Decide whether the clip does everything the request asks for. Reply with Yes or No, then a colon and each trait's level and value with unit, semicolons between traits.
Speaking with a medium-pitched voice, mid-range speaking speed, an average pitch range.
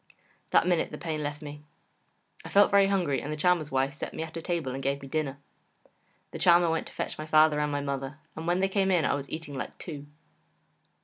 No: medium, 155 Hz; fast, 235 wpm; average, 3.3 semitones